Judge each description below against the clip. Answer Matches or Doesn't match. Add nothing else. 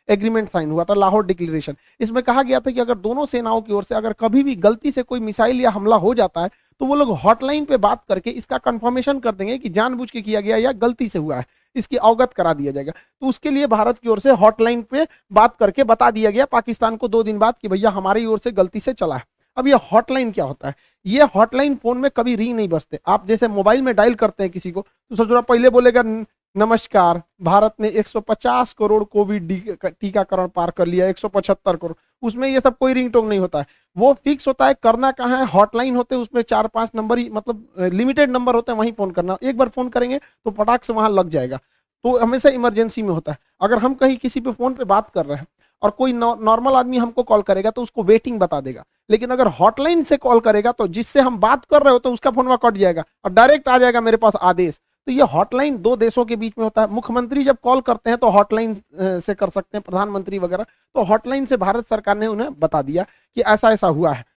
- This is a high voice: Matches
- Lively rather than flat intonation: Doesn't match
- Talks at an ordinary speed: Doesn't match